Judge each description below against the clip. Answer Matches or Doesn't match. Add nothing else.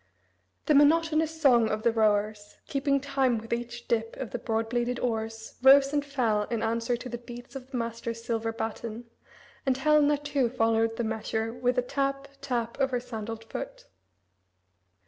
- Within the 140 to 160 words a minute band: Doesn't match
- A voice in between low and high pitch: Doesn't match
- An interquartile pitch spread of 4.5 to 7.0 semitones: Doesn't match